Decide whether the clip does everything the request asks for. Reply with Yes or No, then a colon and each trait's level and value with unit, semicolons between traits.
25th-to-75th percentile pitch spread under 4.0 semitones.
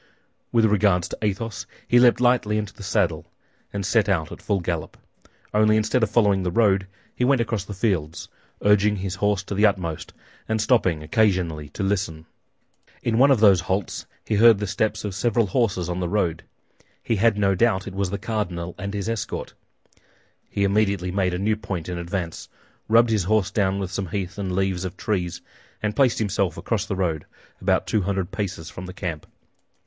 Yes: average, 3.0 semitones